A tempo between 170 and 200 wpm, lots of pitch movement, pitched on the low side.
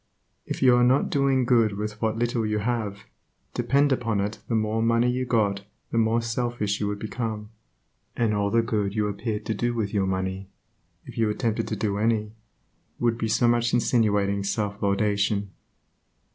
No: average, 180 wpm; narrow, 2.4 semitones; low, 110 Hz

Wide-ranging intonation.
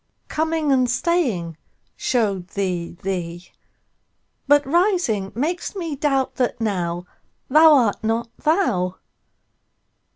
Yes: wide, 8.5 semitones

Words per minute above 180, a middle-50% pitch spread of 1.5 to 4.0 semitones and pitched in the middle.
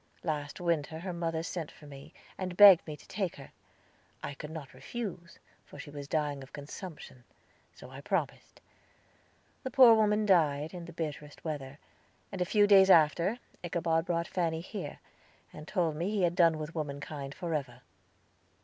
No: average, 165 wpm; average, 3.6 semitones; medium, 165 Hz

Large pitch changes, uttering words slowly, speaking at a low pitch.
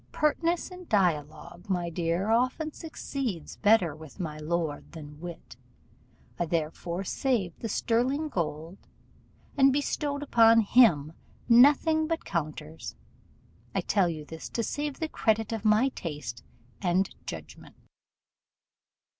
No: wide, 8.3 semitones; slow, 120 wpm; high, 200 Hz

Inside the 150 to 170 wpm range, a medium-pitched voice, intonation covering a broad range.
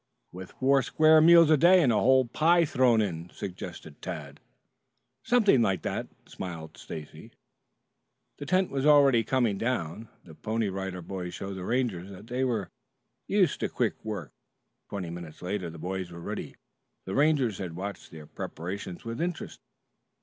No: average, 160 wpm; low, 105 Hz; wide, 6.8 semitones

